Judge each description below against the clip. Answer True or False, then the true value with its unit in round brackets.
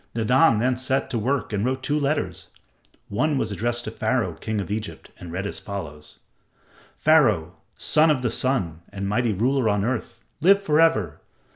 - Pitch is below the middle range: True (120 Hz)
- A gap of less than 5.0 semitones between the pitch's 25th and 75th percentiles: False (5.3 semitones)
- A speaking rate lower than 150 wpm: False (175 wpm)